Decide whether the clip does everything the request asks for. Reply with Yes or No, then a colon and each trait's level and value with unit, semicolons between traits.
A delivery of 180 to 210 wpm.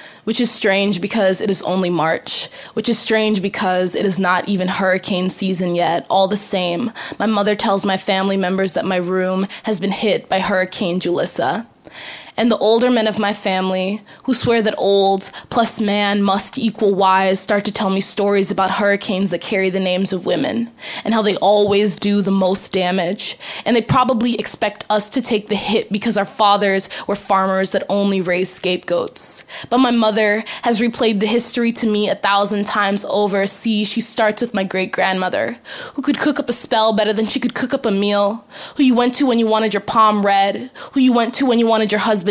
Yes: fast, 205 wpm